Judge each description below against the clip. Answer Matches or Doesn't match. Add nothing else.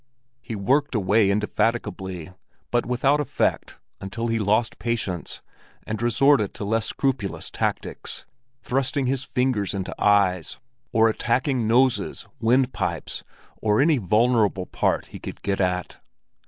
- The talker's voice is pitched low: Matches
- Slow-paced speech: Matches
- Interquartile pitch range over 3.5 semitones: Matches